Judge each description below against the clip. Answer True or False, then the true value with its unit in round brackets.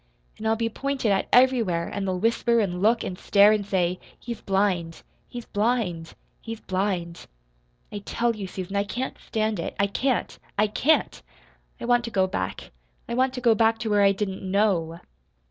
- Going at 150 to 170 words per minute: False (185 wpm)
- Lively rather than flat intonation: False (3.6 semitones)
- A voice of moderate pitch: False (205 Hz)